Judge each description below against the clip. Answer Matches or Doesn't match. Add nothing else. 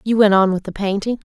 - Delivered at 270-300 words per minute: Matches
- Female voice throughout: Matches